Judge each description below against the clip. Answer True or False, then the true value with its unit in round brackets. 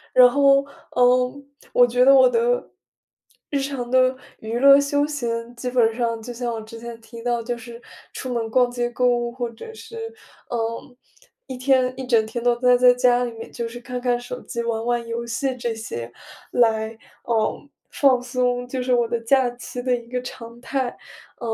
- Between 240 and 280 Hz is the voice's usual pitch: True (245 Hz)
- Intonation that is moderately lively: False (1.5 semitones)